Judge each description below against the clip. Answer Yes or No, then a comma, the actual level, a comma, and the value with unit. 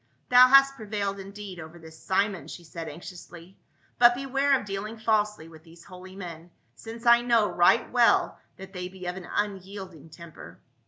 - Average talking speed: Yes, average, 180 wpm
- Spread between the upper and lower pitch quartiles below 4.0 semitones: No, average, 4.4 semitones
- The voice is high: Yes, high, 195 Hz